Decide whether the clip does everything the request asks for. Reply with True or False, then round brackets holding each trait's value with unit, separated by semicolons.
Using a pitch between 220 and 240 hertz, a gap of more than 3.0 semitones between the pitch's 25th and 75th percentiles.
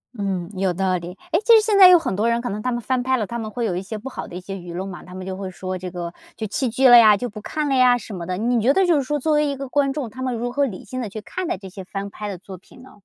True (225 Hz; 5.4 semitones)